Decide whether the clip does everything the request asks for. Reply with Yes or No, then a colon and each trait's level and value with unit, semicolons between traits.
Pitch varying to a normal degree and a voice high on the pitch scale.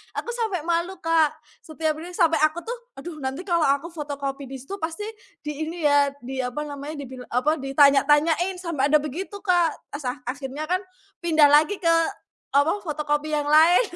Yes: average, 3.0 semitones; very high, 305 Hz